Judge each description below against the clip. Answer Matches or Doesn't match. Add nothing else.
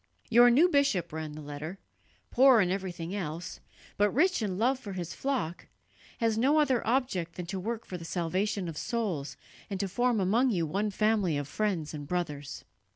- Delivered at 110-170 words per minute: Doesn't match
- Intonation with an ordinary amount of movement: Doesn't match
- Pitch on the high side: Matches